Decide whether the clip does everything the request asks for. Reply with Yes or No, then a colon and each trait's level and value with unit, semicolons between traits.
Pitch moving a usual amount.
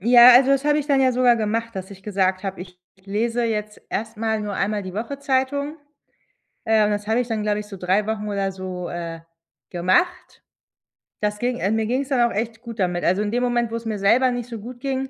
Yes: average, 3.6 semitones